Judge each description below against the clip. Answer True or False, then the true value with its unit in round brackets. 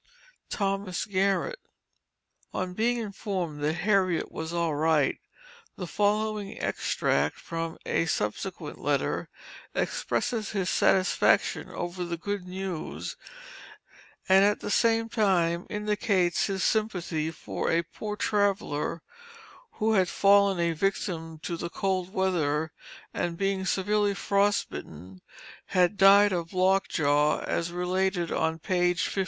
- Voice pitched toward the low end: False (185 Hz)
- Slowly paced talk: True (125 wpm)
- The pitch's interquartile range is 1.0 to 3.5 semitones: True (3.2 semitones)